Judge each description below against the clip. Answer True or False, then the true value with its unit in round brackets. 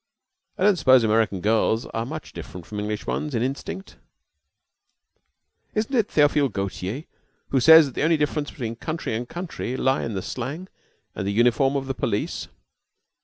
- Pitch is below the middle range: True (130 Hz)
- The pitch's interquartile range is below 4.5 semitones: False (5.4 semitones)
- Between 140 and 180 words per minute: True (170 wpm)